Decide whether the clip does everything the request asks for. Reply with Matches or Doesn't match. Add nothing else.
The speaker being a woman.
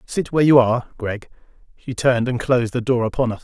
Doesn't match